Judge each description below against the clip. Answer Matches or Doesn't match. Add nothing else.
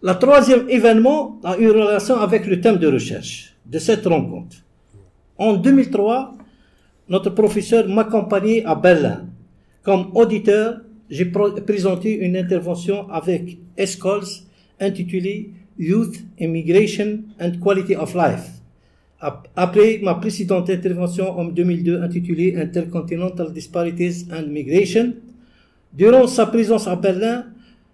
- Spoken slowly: Matches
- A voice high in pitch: Matches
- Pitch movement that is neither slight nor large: Matches